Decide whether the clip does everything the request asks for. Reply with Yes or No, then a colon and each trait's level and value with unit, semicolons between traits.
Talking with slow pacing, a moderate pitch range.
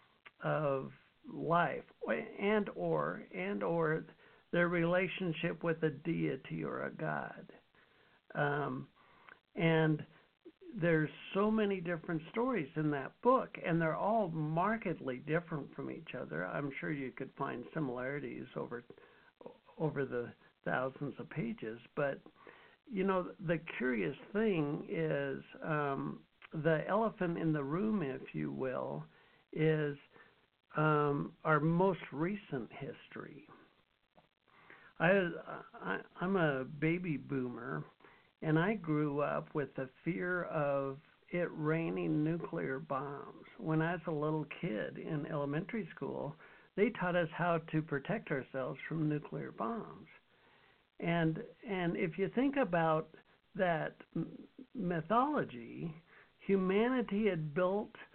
Yes: slow, 120 wpm; average, 4.4 semitones